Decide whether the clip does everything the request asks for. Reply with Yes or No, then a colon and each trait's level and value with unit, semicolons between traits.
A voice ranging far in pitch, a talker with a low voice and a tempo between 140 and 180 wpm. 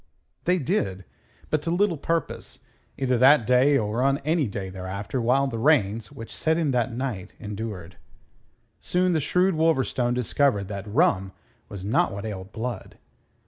Yes: wide, 6.7 semitones; low, 125 Hz; average, 155 wpm